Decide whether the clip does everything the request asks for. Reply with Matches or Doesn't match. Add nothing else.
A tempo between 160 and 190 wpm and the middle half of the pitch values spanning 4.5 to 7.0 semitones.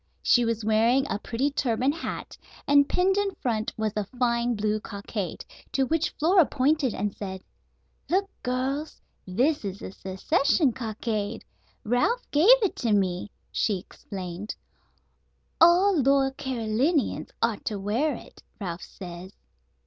Doesn't match